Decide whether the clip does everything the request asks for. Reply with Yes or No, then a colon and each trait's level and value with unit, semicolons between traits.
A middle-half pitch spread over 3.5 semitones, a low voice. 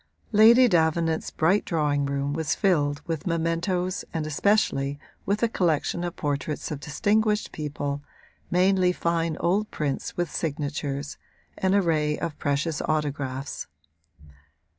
No: average, 4.0 semitones; medium, 160 Hz